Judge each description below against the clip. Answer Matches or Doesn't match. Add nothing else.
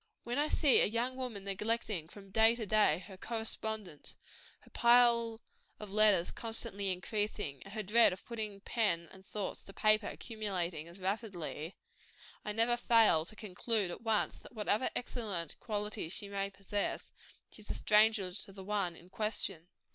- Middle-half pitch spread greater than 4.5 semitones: Doesn't match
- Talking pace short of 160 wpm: Doesn't match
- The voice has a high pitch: Matches